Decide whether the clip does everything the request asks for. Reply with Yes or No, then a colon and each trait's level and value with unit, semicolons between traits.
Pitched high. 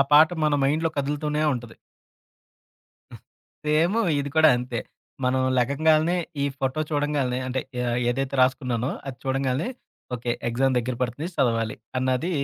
No: low, 135 Hz